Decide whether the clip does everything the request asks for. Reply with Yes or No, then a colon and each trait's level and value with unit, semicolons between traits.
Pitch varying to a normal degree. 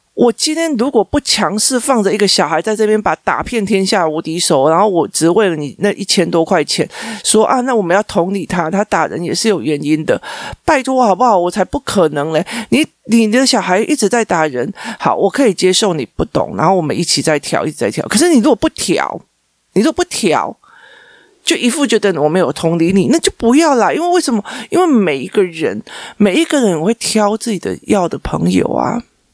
No: wide, 5.8 semitones